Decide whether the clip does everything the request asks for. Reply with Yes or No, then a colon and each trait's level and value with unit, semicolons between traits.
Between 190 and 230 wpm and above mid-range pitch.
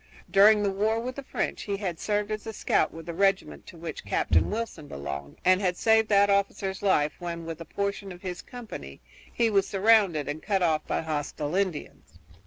Yes: average, 200 wpm; high, 195 Hz